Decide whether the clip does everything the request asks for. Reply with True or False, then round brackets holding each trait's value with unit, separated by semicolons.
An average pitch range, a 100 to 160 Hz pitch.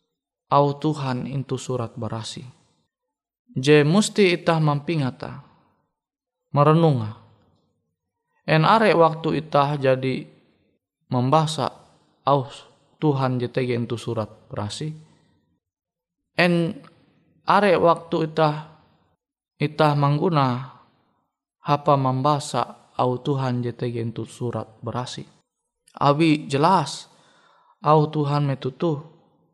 True (4.1 semitones; 140 Hz)